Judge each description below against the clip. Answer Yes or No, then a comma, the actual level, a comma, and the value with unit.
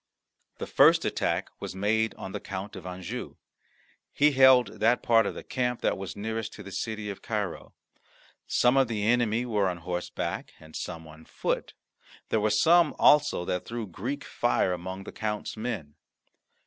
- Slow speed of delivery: No, average, 175 wpm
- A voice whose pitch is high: No, low, 110 Hz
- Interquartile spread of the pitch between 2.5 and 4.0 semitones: No, average, 4.4 semitones